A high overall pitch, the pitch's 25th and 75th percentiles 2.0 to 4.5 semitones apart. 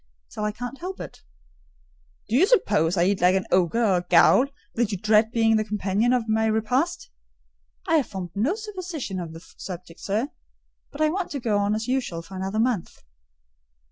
No: high, 220 Hz; average, 5.0 semitones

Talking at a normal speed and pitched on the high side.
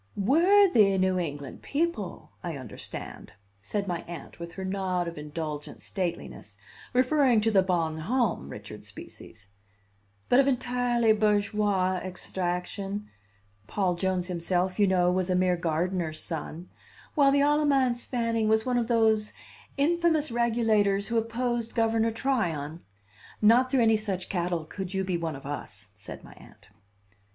Yes: average, 145 wpm; high, 195 Hz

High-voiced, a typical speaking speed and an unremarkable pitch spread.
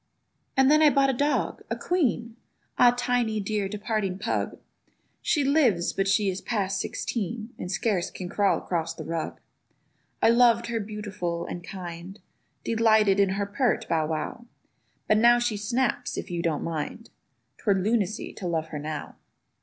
Yes: high, 210 Hz; average, 160 wpm; average, 4.7 semitones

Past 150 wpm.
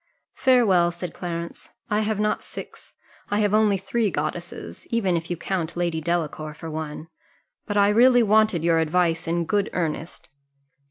Yes: average, 160 wpm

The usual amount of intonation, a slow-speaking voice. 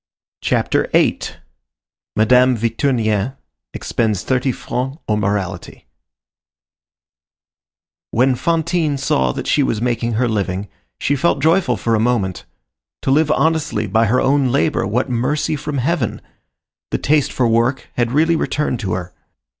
Yes: average, 4.7 semitones; slow, 130 wpm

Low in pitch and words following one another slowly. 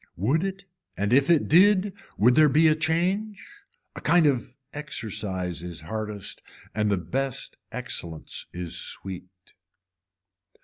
Yes: low, 125 Hz; slow, 130 wpm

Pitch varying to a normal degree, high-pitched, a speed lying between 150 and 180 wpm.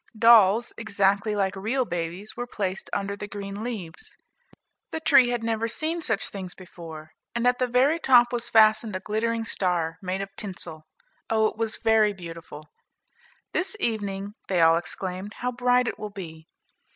Yes: average, 3.9 semitones; high, 210 Hz; average, 165 wpm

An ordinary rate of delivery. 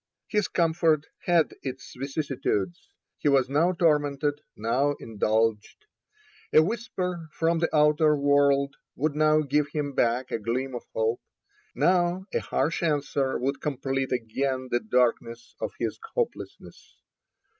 No: slow, 130 wpm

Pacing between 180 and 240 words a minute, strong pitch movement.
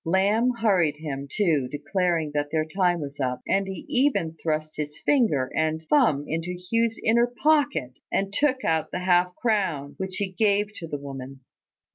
No: average, 170 wpm; wide, 5.8 semitones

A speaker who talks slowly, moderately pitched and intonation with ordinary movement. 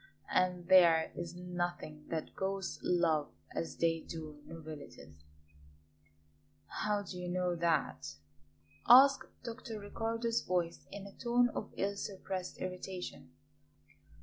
Yes: slow, 120 wpm; medium, 180 Hz; average, 3.8 semitones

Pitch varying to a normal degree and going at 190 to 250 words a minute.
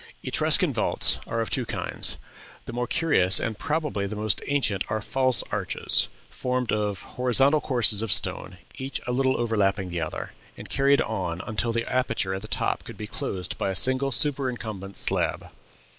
No: average, 4.6 semitones; average, 175 wpm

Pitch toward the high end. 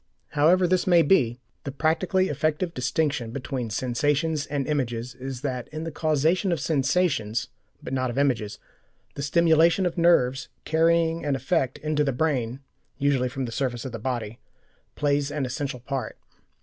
No: medium, 140 Hz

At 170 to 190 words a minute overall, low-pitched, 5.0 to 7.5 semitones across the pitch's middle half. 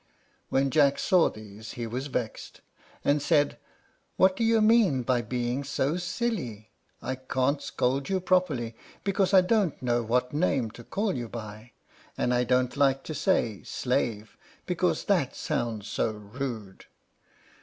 No: average, 150 wpm; low, 130 Hz; wide, 5.5 semitones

